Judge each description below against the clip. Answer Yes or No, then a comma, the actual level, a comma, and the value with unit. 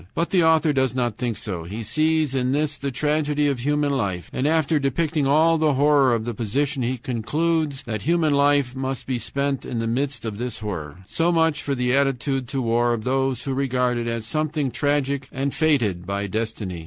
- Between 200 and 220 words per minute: Yes, fast, 205 wpm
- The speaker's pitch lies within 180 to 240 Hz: No, low, 135 Hz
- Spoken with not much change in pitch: No, average, 3.9 semitones